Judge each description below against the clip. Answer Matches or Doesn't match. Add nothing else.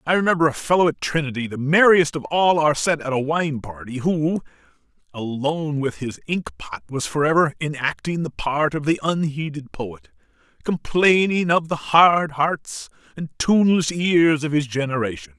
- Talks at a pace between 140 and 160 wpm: Doesn't match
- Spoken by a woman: Doesn't match